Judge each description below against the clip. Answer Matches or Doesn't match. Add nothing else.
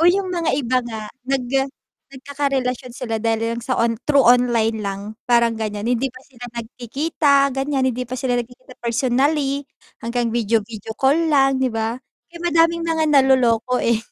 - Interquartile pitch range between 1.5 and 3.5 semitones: Matches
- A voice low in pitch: Doesn't match